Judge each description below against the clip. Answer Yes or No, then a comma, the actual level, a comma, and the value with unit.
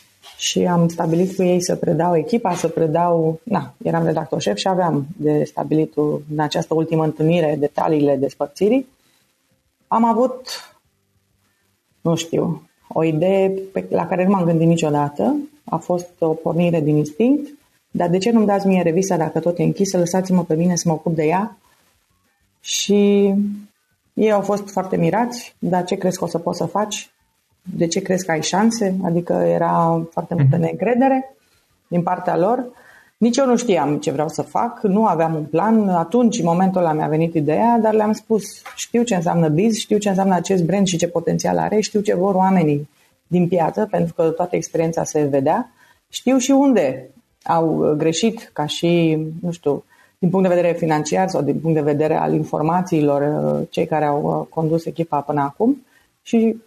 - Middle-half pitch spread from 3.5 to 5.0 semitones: Yes, average, 4.2 semitones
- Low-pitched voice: No, medium, 175 Hz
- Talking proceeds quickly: Yes, fast, 175 wpm